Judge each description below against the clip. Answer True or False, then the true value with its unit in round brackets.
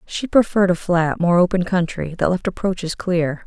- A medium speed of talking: True (190 wpm)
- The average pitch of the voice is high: False (180 Hz)